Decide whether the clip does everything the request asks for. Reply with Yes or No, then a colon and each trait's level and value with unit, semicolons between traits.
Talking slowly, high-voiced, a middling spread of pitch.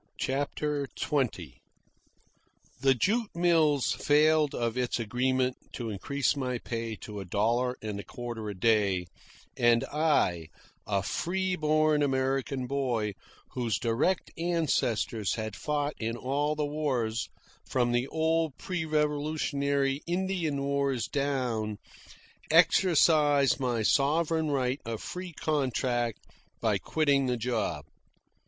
No: slow, 120 wpm; low, 135 Hz; average, 4.5 semitones